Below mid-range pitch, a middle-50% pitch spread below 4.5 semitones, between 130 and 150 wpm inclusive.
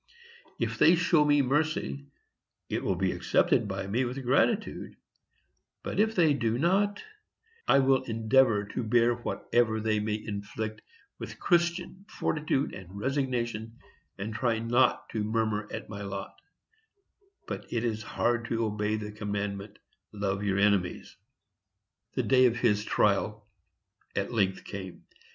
Yes: low, 115 Hz; average, 4.1 semitones; average, 140 wpm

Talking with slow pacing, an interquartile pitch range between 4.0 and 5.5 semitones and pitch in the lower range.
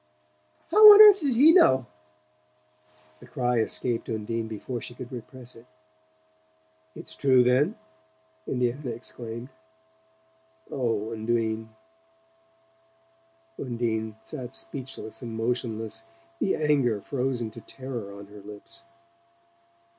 Yes: slow, 110 wpm; average, 4.5 semitones; low, 125 Hz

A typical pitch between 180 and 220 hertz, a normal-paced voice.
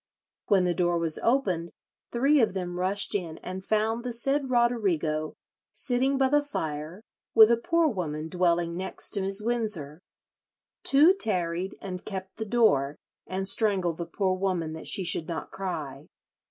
Yes: high, 190 Hz; average, 160 wpm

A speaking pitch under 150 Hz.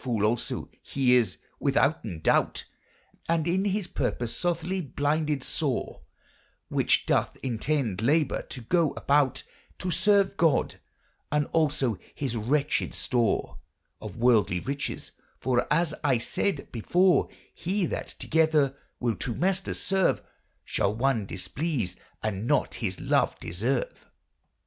Yes: medium, 140 Hz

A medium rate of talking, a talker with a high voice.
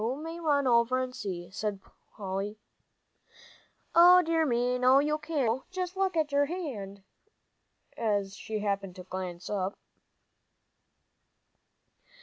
No: slow, 130 wpm; high, 245 Hz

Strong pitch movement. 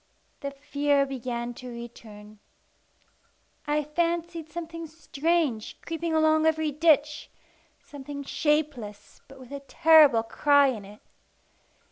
No: average, 4.0 semitones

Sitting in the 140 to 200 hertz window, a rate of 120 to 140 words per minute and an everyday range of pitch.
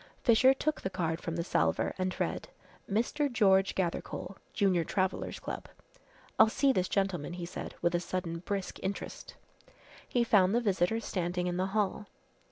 No: high, 190 Hz; average, 165 wpm; average, 3.3 semitones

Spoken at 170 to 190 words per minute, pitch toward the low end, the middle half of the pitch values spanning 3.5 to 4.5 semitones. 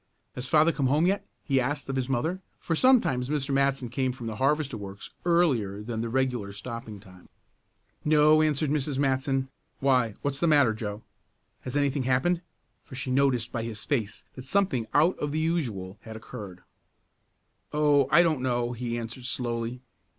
Yes: average, 175 wpm; low, 130 Hz; average, 4.1 semitones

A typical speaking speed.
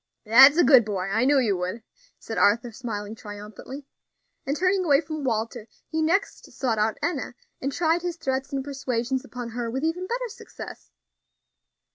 Yes: average, 170 wpm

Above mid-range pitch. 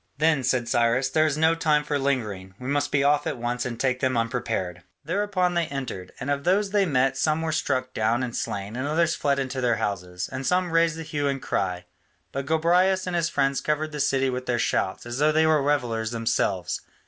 No: low, 135 Hz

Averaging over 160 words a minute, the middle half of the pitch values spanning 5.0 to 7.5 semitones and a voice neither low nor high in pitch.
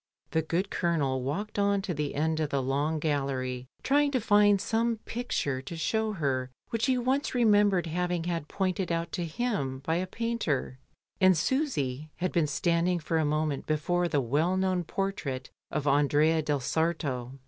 Yes: average, 170 wpm; average, 5.3 semitones; medium, 165 Hz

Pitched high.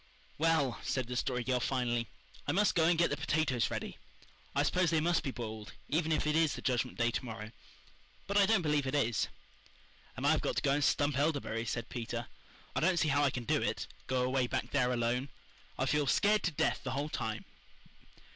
No: low, 135 Hz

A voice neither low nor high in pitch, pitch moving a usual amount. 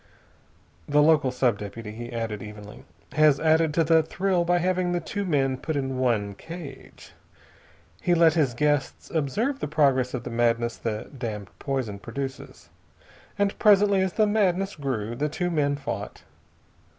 No: medium, 145 Hz; wide, 6.3 semitones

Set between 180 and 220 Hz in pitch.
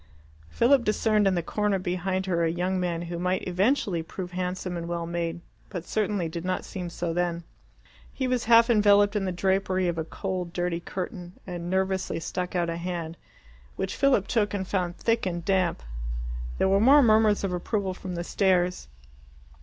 Yes: medium, 185 Hz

